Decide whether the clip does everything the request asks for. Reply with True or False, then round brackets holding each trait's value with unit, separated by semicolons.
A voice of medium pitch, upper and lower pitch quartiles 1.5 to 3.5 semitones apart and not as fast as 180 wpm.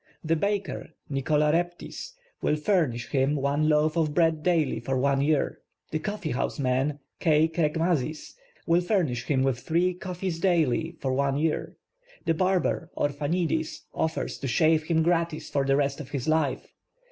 True (155 Hz; 3.2 semitones; 160 wpm)